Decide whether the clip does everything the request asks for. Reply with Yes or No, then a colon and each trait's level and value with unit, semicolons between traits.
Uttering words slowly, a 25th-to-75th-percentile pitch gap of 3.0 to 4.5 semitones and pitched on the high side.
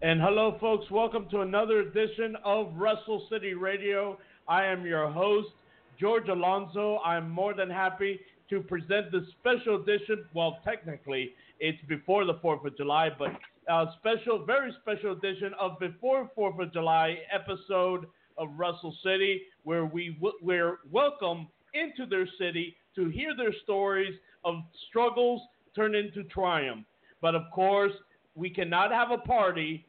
No: average, 150 wpm; average, 3.9 semitones; high, 195 Hz